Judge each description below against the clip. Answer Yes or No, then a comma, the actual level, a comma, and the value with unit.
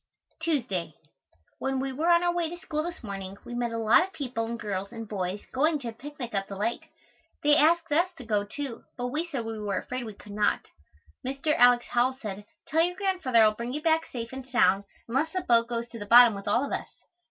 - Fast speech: Yes, fast, 240 wpm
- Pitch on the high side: Yes, high, 245 Hz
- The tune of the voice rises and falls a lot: Yes, wide, 5.8 semitones